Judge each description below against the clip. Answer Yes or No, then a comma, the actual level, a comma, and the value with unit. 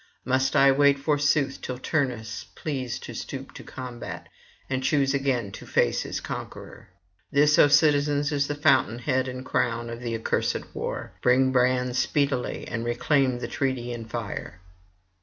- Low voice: Yes, low, 130 Hz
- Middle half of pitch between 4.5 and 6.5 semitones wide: No, average, 2.7 semitones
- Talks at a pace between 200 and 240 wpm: No, average, 160 wpm